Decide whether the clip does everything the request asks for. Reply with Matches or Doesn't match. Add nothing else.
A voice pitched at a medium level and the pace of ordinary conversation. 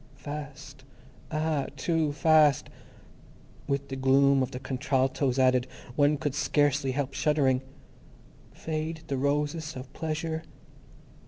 Doesn't match